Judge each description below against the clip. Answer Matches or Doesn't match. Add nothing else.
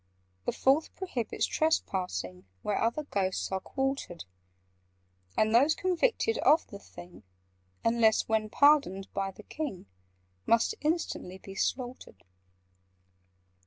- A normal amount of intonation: Doesn't match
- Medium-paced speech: Doesn't match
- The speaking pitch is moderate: Doesn't match